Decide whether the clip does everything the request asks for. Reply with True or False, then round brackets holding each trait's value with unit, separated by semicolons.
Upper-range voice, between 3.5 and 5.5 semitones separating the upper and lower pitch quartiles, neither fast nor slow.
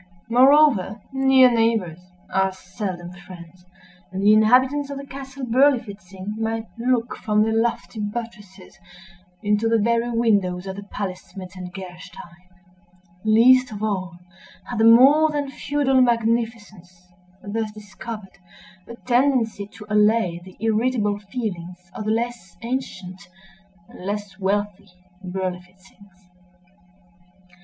False (210 Hz; 4.0 semitones; 115 wpm)